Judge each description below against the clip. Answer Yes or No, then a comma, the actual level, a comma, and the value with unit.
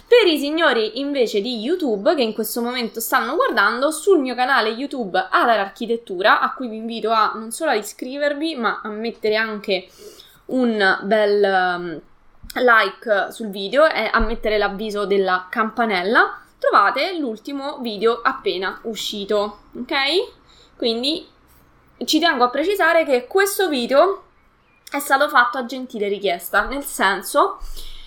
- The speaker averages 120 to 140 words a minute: Yes, average, 135 wpm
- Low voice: No, high, 240 Hz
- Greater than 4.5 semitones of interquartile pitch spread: Yes, wide, 5.5 semitones